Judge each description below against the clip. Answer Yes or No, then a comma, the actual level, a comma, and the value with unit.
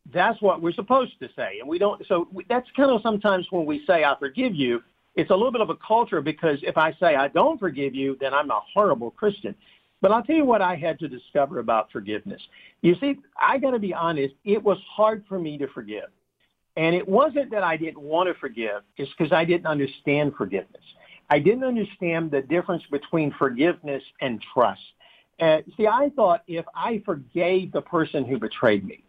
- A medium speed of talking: No, fast, 210 wpm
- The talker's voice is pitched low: No, medium, 170 Hz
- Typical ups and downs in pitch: No, wide, 6.4 semitones